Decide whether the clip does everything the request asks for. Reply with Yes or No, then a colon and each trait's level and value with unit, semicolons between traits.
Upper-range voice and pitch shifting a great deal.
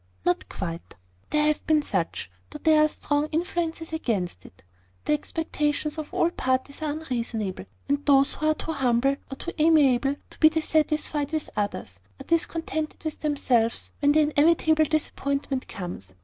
No: very high, 295 Hz; average, 3.3 semitones